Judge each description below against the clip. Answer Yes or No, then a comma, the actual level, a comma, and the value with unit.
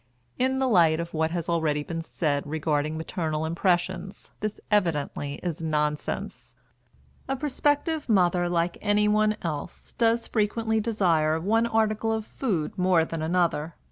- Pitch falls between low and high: Yes, medium, 175 Hz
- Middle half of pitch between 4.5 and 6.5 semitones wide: Yes, average, 5.1 semitones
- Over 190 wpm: No, average, 140 wpm